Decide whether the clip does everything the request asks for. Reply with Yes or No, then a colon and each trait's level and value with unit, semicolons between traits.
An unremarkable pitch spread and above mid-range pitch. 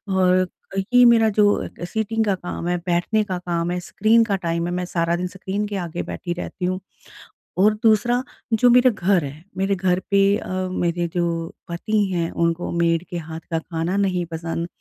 No: average, 3.2 semitones; medium, 180 Hz